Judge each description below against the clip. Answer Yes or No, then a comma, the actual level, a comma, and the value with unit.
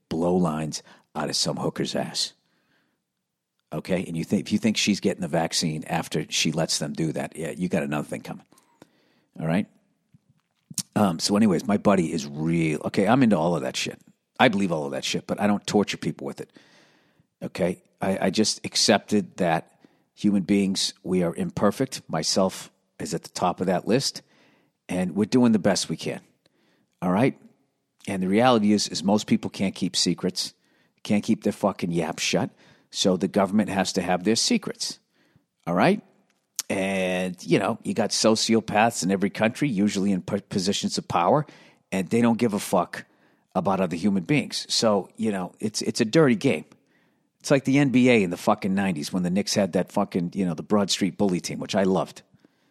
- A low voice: Yes, low, 100 Hz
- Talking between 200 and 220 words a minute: No, average, 190 wpm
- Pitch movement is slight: No, average, 3.2 semitones